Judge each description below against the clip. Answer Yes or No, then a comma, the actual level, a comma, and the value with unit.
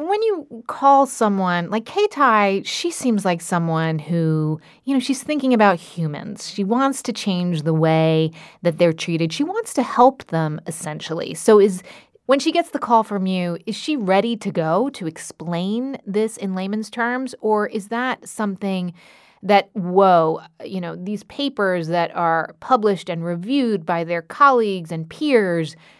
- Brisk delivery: No, average, 165 wpm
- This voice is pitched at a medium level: No, high, 195 Hz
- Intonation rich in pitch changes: Yes, wide, 6.2 semitones